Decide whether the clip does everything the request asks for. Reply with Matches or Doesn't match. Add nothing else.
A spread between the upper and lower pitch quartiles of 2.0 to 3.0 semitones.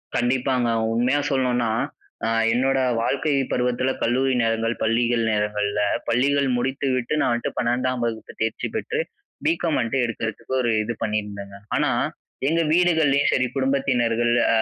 Matches